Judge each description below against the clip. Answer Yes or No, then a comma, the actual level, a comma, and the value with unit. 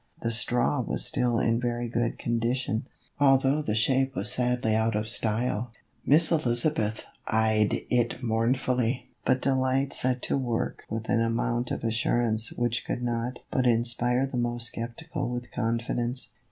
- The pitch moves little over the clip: Yes, narrow, 1.8 semitones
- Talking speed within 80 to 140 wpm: No, average, 155 wpm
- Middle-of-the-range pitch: No, low, 120 Hz